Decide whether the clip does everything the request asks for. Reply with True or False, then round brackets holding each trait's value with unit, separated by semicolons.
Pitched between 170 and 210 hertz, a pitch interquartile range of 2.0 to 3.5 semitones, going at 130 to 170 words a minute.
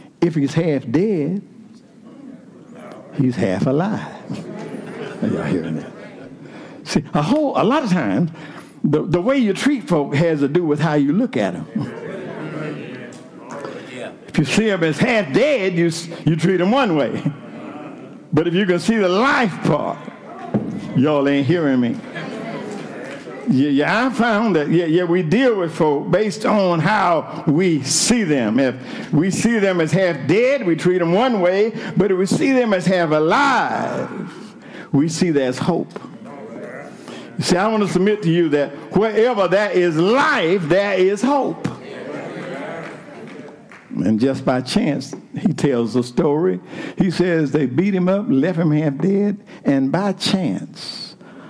False (185 Hz; 5.0 semitones; 155 wpm)